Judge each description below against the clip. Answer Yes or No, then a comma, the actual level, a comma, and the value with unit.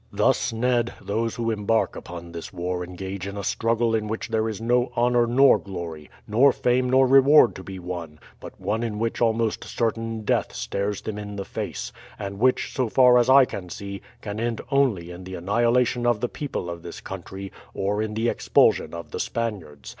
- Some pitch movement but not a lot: Yes, average, 3.8 semitones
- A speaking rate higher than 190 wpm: Yes, average, 200 wpm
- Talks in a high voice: No, low, 110 Hz